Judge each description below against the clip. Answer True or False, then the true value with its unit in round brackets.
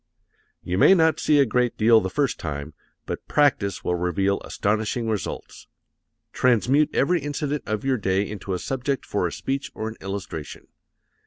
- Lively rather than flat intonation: True (5.9 semitones)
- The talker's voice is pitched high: False (110 Hz)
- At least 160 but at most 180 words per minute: True (165 wpm)